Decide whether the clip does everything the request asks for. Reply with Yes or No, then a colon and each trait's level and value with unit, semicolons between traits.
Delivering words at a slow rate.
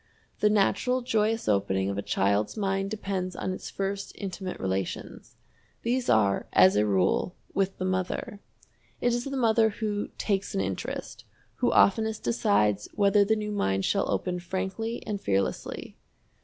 No: average, 155 wpm